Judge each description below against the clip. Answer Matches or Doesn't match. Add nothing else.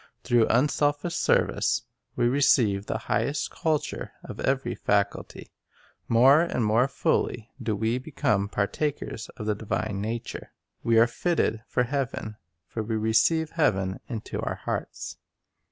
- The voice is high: Doesn't match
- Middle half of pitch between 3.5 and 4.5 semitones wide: Matches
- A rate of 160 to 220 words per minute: Doesn't match